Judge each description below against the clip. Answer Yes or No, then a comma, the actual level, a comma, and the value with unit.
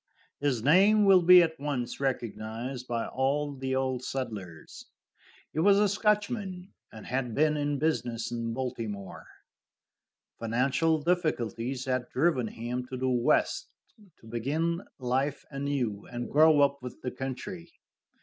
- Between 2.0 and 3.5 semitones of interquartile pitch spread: No, average, 4.7 semitones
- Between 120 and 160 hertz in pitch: Yes, low, 135 Hz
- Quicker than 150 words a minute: No, slow, 135 wpm